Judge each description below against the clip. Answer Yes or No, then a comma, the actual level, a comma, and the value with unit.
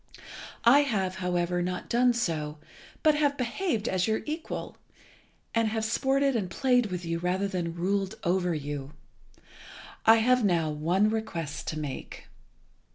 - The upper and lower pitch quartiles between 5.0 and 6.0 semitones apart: Yes, wide, 5.5 semitones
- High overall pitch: Yes, high, 195 Hz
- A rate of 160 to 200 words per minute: No, average, 145 wpm